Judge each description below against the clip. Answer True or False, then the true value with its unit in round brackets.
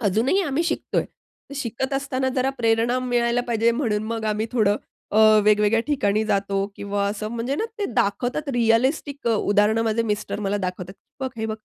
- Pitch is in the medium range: False (225 Hz)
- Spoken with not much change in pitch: False (3.4 semitones)